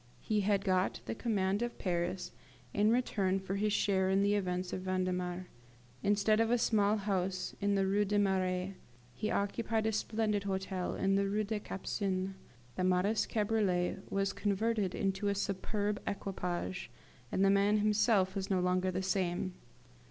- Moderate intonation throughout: No, narrow, 1.9 semitones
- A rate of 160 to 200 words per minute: Yes, average, 165 wpm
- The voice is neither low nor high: No, high, 195 Hz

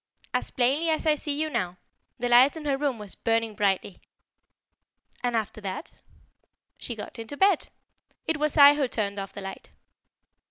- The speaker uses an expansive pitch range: Yes, wide, 5.9 semitones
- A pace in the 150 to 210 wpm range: Yes, average, 170 wpm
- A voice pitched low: No, high, 245 Hz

